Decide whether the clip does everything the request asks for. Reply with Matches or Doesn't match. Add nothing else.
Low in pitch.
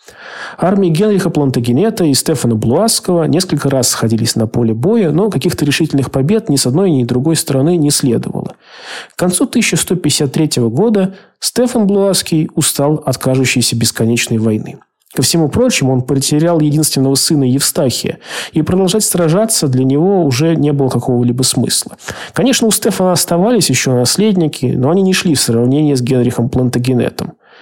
Doesn't match